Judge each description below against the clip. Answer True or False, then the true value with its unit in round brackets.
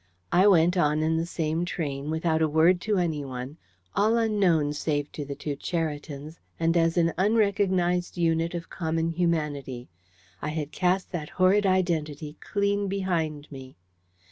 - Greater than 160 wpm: False (150 wpm)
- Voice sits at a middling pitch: True (165 Hz)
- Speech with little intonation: False (3.2 semitones)